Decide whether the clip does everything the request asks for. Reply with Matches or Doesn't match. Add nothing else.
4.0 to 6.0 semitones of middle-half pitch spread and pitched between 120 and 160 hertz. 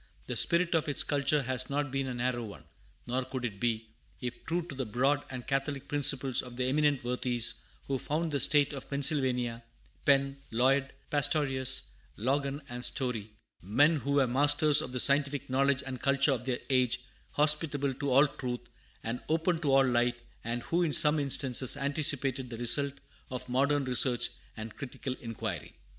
Doesn't match